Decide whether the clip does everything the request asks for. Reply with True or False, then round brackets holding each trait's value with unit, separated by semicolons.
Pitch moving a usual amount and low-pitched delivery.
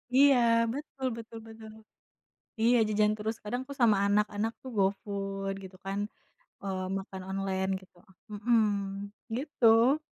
False (3.2 semitones; 215 Hz)